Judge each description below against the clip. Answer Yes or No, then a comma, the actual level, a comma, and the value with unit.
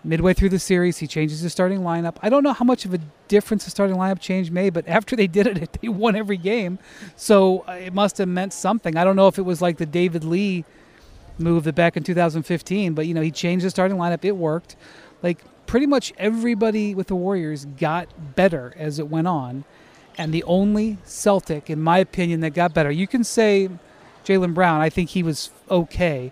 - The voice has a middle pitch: Yes, medium, 180 Hz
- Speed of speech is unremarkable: No, fast, 215 wpm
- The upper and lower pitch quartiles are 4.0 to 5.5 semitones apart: No, average, 2.8 semitones